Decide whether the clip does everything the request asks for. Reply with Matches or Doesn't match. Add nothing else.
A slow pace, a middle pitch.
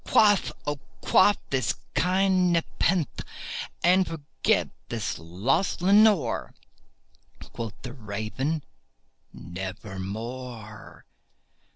Doesn't match